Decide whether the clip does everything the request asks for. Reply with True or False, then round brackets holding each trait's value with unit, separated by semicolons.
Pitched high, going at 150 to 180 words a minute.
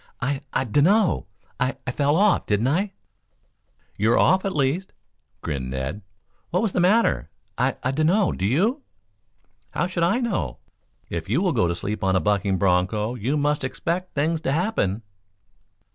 False (140 Hz; 165 wpm)